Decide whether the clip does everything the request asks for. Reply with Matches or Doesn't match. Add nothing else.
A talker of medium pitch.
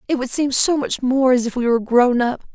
Doesn't match